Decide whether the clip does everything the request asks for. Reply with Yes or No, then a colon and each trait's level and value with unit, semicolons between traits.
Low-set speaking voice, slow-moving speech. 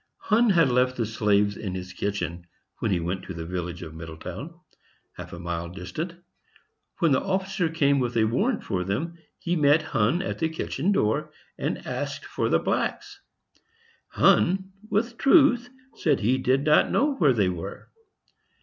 No: low, 130 Hz; average, 170 wpm